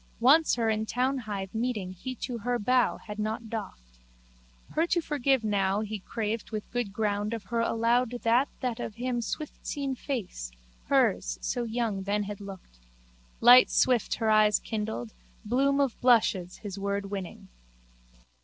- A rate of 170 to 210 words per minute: No, average, 155 wpm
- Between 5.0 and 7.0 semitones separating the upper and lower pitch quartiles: No, average, 3.4 semitones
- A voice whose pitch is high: Yes, high, 220 Hz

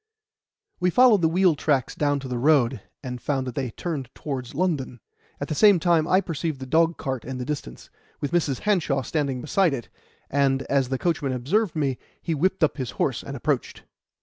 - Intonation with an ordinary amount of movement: Yes, average, 4.4 semitones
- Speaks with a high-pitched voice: No, medium, 145 Hz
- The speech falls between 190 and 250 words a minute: Yes, average, 195 wpm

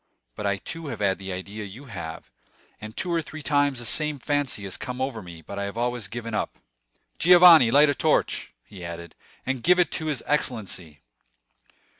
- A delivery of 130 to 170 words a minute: No, average, 200 wpm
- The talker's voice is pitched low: Yes, low, 120 Hz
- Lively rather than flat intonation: Yes, wide, 6.5 semitones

